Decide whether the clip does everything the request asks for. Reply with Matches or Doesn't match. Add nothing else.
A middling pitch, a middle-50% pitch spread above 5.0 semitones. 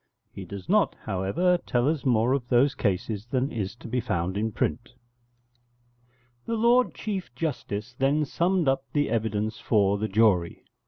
Doesn't match